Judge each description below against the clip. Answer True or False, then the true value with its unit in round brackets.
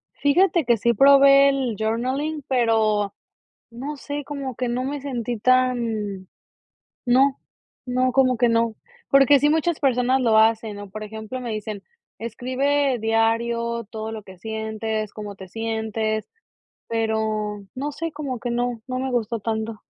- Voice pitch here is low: False (235 Hz)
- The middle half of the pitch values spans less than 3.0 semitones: False (3.3 semitones)